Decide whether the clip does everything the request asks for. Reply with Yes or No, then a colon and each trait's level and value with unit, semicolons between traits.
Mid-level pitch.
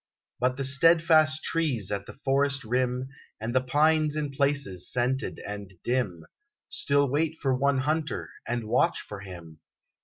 No: low, 130 Hz